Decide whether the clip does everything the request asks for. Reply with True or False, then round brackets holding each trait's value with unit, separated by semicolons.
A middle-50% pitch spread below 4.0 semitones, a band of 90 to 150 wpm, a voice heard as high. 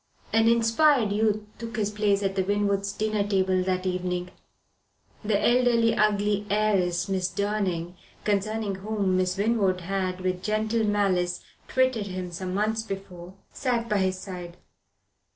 True (2.6 semitones; 140 wpm; 200 Hz)